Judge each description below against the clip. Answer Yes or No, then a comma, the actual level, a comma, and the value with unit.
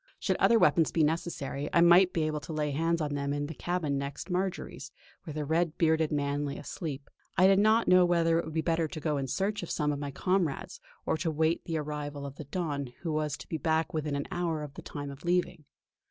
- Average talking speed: No, fast, 240 wpm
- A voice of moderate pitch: Yes, medium, 155 Hz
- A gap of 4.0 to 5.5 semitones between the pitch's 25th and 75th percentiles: No, average, 2.8 semitones